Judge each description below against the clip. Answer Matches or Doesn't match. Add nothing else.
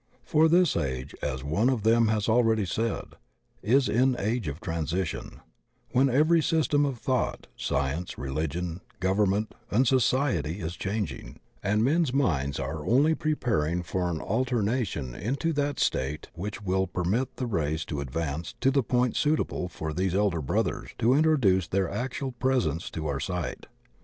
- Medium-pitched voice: Doesn't match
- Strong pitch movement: Matches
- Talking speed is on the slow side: Doesn't match